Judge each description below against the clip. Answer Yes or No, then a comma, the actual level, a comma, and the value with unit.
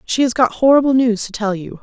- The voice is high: Yes, high, 235 Hz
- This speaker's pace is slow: No, fast, 265 wpm